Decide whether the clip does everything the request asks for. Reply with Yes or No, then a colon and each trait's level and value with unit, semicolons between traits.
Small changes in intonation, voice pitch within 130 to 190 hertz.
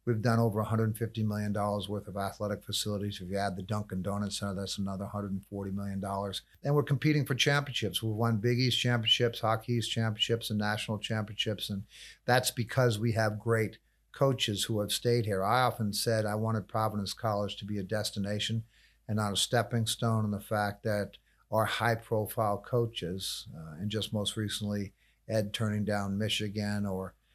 No: narrow, 2.0 semitones; low, 105 Hz